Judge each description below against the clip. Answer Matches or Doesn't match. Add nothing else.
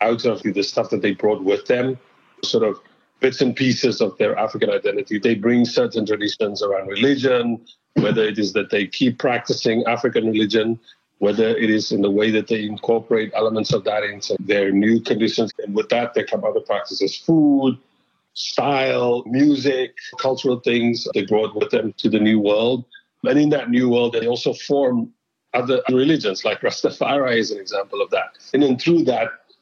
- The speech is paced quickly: Doesn't match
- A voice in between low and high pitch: Doesn't match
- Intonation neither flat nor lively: Matches